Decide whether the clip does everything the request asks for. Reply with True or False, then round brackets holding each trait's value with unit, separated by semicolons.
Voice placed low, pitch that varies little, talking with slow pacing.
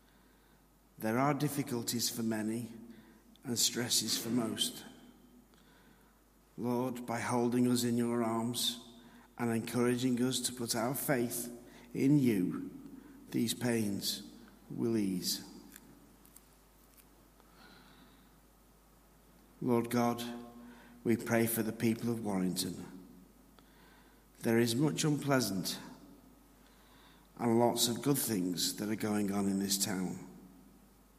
True (120 Hz; 1.6 semitones; 105 wpm)